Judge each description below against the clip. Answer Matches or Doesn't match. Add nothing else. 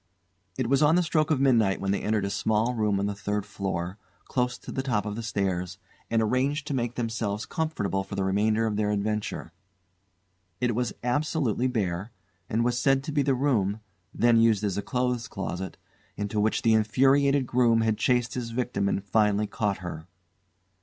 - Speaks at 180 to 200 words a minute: Matches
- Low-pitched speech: Matches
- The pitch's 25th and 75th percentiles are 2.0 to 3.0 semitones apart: Doesn't match